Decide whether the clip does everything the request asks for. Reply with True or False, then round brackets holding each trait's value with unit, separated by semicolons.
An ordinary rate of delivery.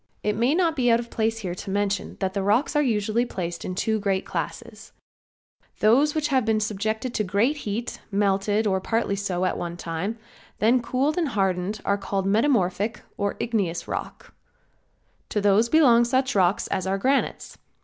True (175 wpm)